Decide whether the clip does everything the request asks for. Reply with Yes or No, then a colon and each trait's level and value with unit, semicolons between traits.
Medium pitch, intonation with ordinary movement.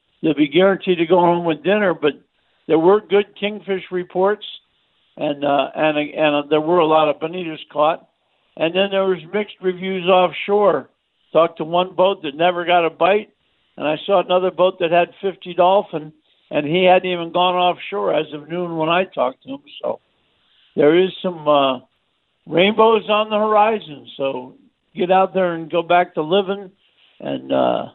Yes: medium, 180 Hz; average, 3.4 semitones